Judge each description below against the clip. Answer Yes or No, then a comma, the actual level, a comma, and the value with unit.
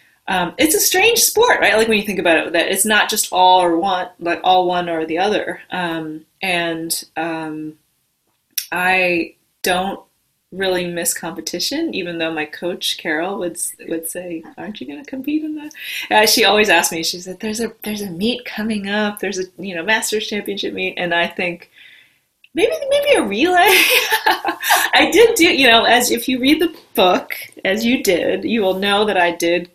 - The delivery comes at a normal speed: Yes, average, 190 wpm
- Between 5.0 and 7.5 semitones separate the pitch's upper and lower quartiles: Yes, wide, 5.6 semitones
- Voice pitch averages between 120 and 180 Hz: No, high, 190 Hz